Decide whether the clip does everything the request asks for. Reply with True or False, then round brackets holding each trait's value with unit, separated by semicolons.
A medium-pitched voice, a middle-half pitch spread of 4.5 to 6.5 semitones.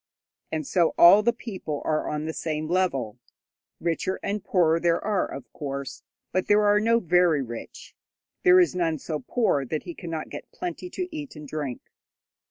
True (170 Hz; 5.3 semitones)